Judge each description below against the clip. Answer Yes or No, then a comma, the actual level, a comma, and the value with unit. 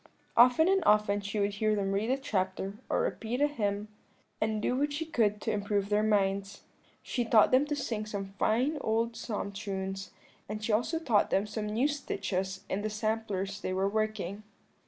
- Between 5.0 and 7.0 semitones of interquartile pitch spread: No, average, 2.7 semitones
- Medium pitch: No, high, 210 Hz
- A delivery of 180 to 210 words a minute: Yes, average, 190 wpm